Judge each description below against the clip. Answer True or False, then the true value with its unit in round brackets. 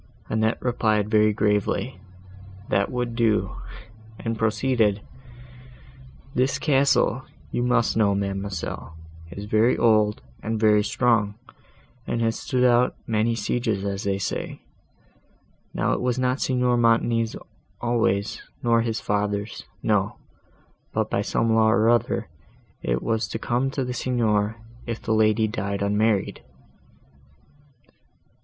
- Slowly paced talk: True (120 wpm)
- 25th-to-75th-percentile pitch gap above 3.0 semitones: False (2.7 semitones)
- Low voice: True (110 Hz)